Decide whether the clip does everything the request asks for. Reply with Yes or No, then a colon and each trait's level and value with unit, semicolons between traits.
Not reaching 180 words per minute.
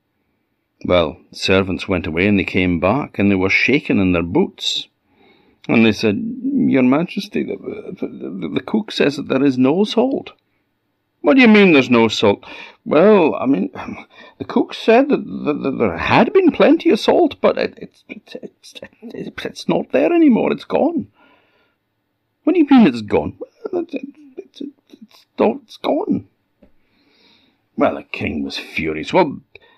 Yes: average, 170 wpm